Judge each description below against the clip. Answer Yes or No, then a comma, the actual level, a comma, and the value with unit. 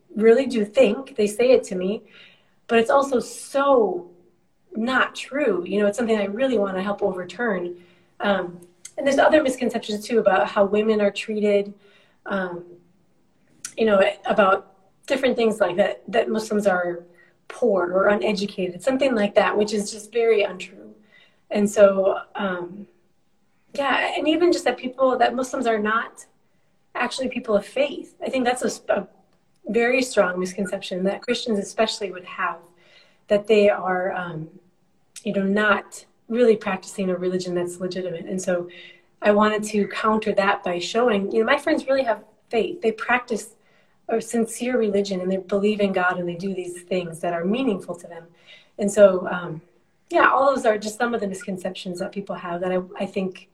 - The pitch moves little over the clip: No, average, 3.7 semitones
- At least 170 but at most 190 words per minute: Yes, average, 175 wpm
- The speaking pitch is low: No, high, 205 Hz